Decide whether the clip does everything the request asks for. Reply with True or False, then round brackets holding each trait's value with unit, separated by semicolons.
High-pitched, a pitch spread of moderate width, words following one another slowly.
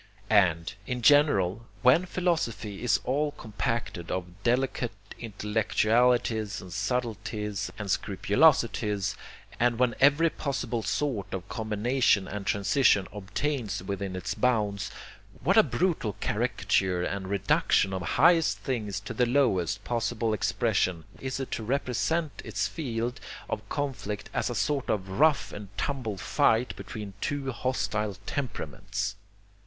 False (110 Hz; 4.2 semitones; 125 wpm)